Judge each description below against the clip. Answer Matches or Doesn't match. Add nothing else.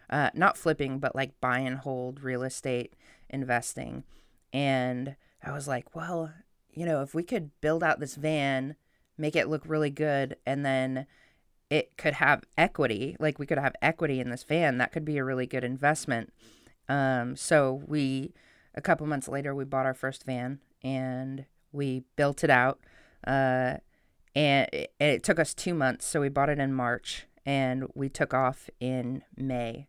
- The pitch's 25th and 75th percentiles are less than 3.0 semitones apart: Matches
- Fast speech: Doesn't match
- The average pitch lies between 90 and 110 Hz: Doesn't match